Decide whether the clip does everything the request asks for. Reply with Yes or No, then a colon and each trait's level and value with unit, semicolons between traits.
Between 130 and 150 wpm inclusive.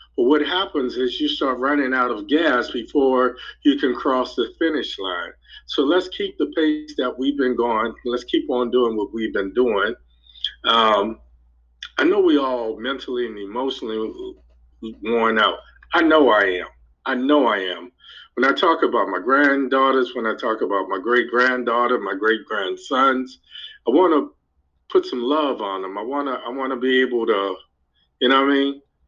No: average, 180 wpm